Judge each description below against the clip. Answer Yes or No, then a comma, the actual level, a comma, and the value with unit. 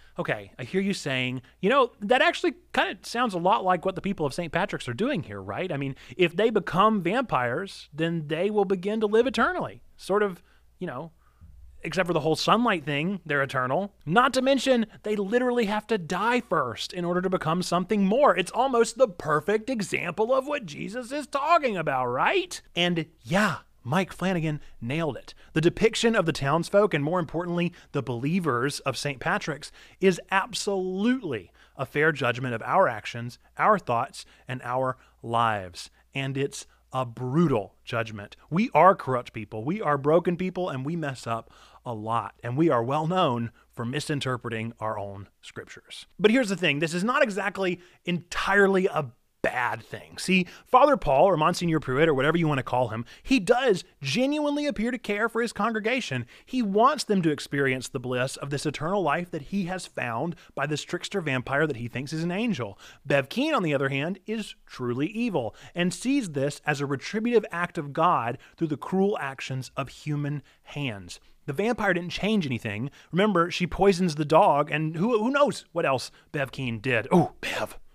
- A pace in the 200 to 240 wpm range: No, average, 185 wpm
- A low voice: No, medium, 170 Hz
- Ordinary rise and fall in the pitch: No, wide, 6.9 semitones